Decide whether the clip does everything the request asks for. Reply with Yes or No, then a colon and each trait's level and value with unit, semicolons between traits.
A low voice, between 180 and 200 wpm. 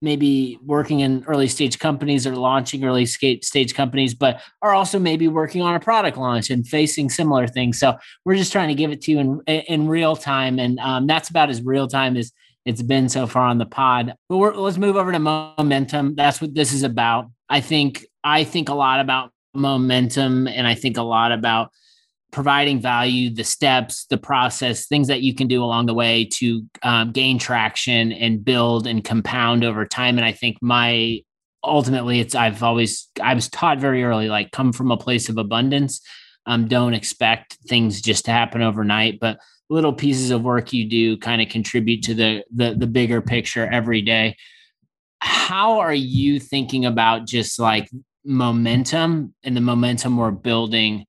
Yes: low, 125 Hz; average, 190 wpm